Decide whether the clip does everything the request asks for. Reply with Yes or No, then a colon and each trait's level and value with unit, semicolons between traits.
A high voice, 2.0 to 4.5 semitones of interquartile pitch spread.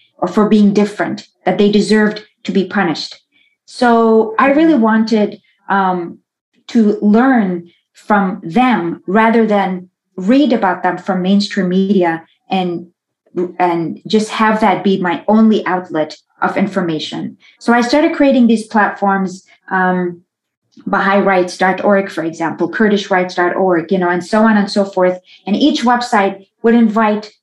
Yes: high, 200 Hz; average, 3.1 semitones